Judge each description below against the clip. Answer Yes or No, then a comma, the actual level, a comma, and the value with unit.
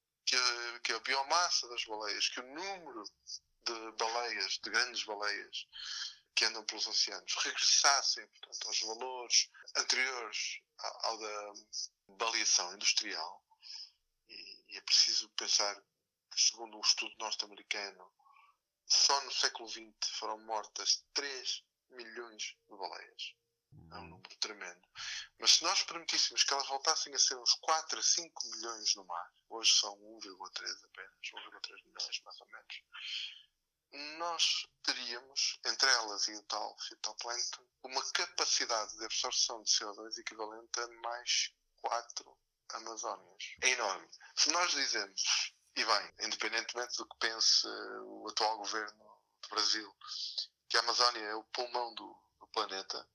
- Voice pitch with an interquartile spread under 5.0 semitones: Yes, average, 4.1 semitones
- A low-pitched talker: Yes, low, 120 Hz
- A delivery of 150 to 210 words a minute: No, average, 135 wpm